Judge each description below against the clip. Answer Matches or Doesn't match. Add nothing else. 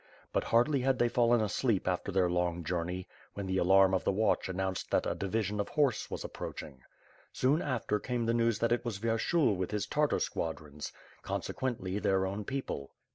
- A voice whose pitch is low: Matches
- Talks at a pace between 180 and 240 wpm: Matches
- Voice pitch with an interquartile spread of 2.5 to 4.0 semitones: Doesn't match